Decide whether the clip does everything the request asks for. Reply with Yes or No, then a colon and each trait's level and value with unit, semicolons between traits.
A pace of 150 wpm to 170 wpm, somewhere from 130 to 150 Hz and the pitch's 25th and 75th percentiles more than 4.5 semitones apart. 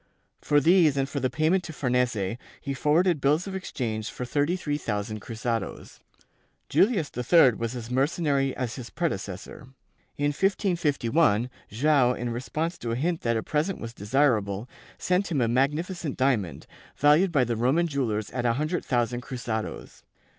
Yes: average, 160 wpm; low, 135 Hz; average, 5.1 semitones